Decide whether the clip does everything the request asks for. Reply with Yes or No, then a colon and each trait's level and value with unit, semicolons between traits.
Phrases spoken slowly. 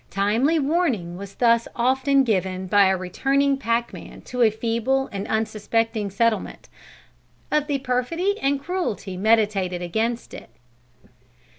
Yes: slow, 125 wpm